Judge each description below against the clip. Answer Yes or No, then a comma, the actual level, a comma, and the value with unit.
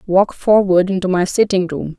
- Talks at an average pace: Yes, average, 180 wpm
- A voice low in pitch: No, medium, 185 Hz